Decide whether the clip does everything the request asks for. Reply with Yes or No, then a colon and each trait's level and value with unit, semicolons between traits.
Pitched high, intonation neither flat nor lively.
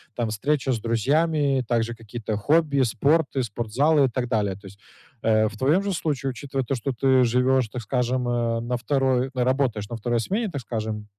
No: low, 125 Hz; average, 3.3 semitones